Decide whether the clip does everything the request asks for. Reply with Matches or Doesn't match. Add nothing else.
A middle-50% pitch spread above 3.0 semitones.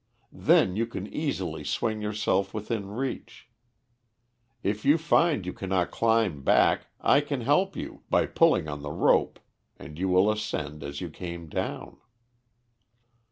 Matches